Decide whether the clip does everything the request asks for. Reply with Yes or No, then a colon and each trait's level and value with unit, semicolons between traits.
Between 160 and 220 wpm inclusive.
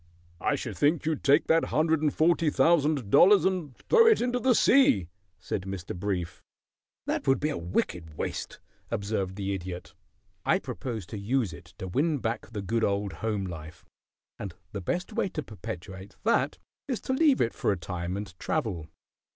Yes: average, 175 wpm